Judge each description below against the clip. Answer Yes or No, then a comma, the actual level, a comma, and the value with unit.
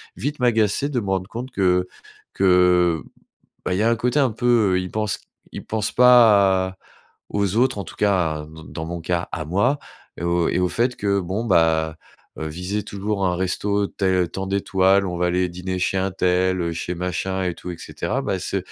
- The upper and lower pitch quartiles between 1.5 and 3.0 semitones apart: Yes, narrow, 2.6 semitones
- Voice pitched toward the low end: Yes, very low, 95 Hz